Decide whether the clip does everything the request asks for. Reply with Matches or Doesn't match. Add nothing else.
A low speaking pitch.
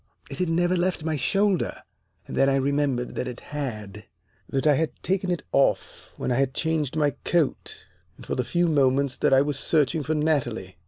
Doesn't match